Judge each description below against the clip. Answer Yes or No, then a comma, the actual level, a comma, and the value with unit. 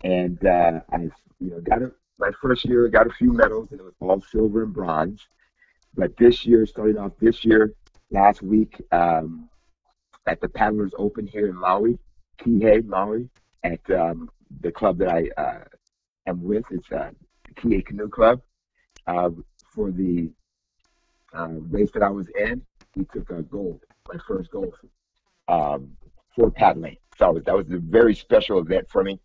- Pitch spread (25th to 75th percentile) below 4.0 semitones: No, average, 4.3 semitones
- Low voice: Yes, low, 100 Hz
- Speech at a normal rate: Yes, average, 175 wpm